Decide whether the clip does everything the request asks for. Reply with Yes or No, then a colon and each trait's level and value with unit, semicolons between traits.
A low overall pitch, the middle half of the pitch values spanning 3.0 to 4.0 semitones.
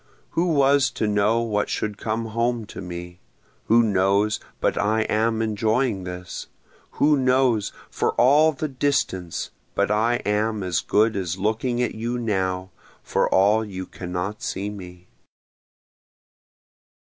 Yes: low, 110 Hz; average, 3.7 semitones